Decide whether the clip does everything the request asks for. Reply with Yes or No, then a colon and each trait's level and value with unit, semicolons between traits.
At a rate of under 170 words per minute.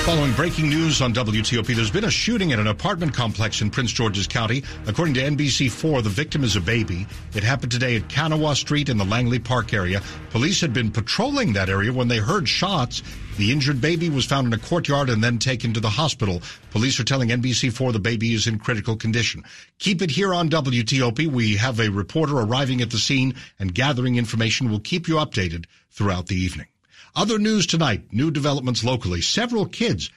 No: average, 200 wpm